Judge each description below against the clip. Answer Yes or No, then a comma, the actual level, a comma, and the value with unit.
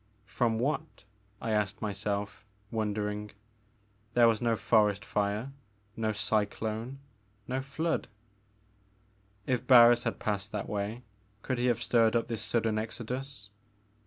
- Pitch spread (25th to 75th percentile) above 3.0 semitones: No, narrow, 2.5 semitones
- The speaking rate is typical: No, slow, 125 wpm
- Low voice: Yes, low, 110 Hz